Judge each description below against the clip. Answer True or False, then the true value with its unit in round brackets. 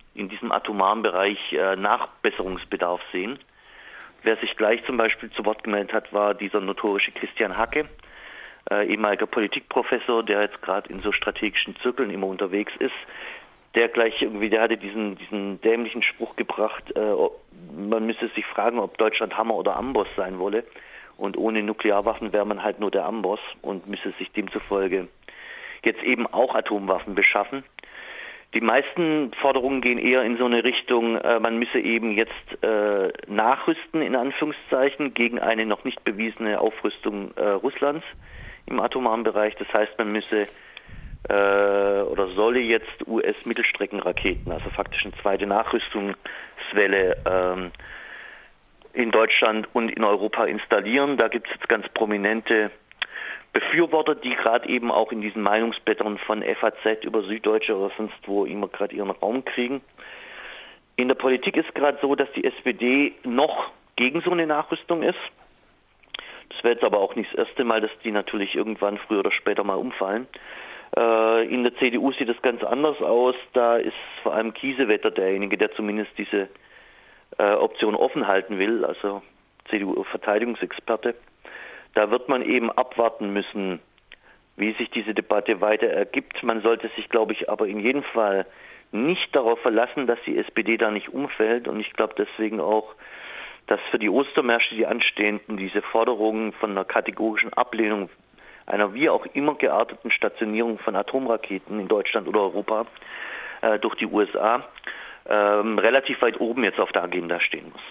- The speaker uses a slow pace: False (155 wpm)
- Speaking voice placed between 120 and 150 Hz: False (110 Hz)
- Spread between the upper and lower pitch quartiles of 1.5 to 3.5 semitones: True (3.0 semitones)